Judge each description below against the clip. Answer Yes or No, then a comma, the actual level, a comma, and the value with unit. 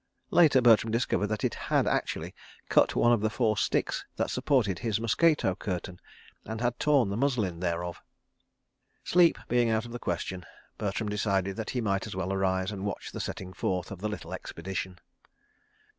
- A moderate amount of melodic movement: Yes, average, 3.9 semitones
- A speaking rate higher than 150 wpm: Yes, average, 175 wpm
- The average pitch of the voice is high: No, low, 105 Hz